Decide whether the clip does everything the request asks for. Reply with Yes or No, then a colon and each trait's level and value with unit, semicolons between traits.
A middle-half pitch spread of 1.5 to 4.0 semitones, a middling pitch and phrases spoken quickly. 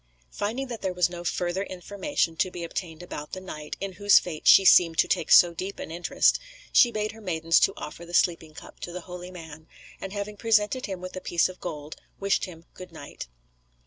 Yes: average, 3.1 semitones; medium, 180 Hz; fast, 215 wpm